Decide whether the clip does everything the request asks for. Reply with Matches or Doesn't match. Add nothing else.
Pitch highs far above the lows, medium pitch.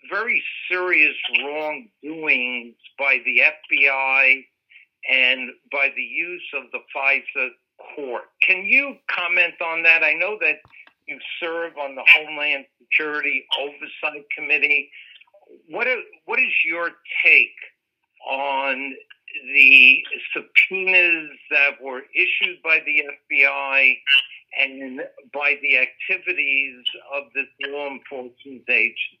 Doesn't match